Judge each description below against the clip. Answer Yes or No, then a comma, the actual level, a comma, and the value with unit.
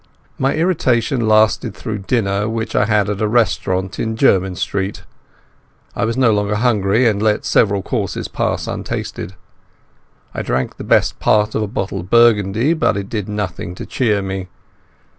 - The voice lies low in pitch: Yes, low, 105 Hz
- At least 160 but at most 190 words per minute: Yes, average, 165 wpm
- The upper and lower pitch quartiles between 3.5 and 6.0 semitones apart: No, average, 2.7 semitones